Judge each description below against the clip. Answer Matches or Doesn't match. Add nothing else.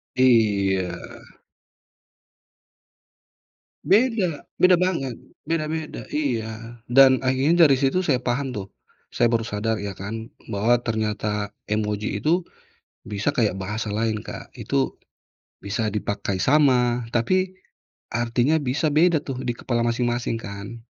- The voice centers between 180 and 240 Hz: Doesn't match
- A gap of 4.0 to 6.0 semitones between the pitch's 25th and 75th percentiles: Matches